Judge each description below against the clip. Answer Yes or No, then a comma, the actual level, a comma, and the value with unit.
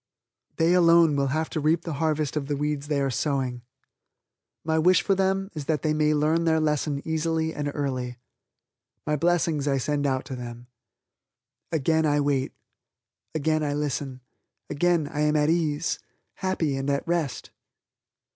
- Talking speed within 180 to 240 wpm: No, average, 165 wpm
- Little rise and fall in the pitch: Yes, narrow, 2.3 semitones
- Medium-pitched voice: Yes, medium, 150 Hz